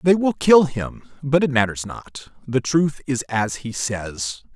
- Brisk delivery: No, average, 185 wpm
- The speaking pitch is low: Yes, low, 130 Hz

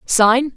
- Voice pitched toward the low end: No, high, 245 Hz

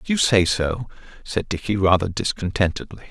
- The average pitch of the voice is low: Yes, low, 100 Hz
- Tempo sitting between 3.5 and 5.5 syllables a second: Yes, 5.4 syllables/s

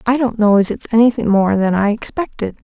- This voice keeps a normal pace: No, fast, 220 wpm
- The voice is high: Yes, high, 220 Hz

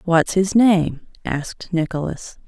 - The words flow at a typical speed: No, slow, 120 wpm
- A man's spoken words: No, female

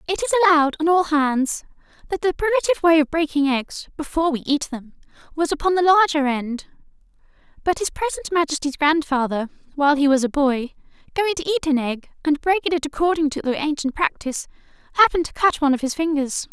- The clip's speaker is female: Yes, female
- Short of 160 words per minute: No, average, 190 wpm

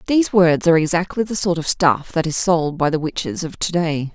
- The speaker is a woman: Yes, female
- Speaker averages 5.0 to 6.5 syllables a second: Yes, 5.5 syllables/s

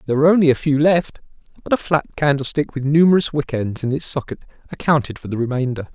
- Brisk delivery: Yes, fast, 210 wpm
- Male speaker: Yes, male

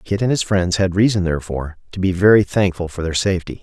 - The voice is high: No, very low, 90 Hz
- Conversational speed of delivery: No, fast, 230 wpm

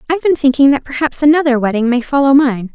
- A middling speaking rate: No, fast, 220 wpm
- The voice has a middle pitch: No, very high, 270 Hz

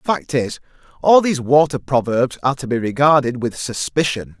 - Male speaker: Yes, male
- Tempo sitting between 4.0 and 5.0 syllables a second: No, 5.2 syllables/s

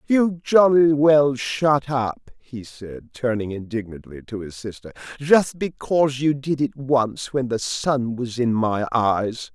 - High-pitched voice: No, low, 130 Hz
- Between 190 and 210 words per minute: No, average, 155 wpm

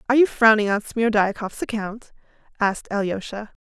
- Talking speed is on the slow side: Yes, slow, 130 wpm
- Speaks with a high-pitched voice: Yes, high, 215 Hz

